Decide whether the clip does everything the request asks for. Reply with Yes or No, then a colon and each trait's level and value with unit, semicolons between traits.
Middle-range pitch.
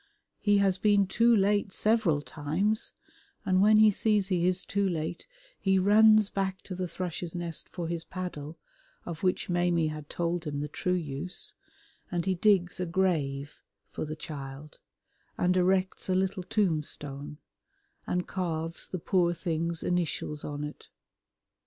Yes: medium, 180 Hz